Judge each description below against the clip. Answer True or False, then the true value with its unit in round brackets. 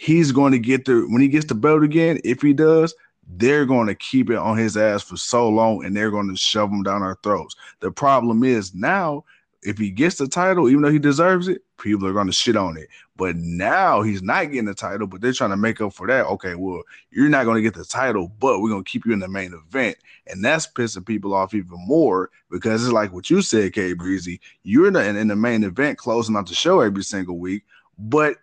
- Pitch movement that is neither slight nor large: False (6.0 semitones)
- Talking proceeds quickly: True (250 wpm)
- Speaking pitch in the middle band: False (110 Hz)